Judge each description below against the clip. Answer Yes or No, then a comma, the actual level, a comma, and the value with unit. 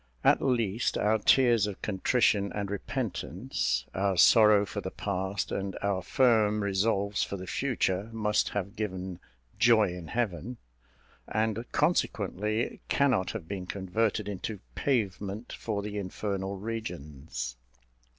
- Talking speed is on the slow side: Yes, slow, 125 wpm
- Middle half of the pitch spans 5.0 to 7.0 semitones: No, average, 2.8 semitones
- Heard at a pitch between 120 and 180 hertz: No, low, 100 Hz